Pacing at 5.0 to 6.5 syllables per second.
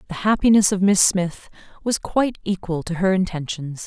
Yes: 5.2 syllables/s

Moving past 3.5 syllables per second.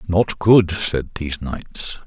No: 3.2 syllables/s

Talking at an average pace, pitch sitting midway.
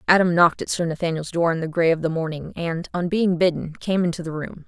No: fast, 255 wpm; medium, 170 Hz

